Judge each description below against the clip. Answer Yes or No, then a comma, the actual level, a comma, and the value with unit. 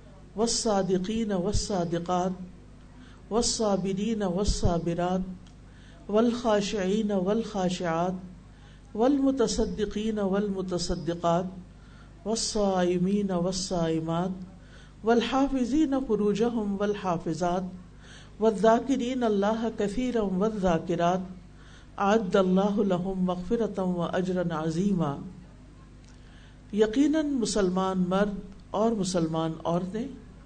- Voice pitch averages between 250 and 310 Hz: No, high, 195 Hz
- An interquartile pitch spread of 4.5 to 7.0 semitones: No, average, 3.4 semitones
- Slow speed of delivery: Yes, slow, 80 wpm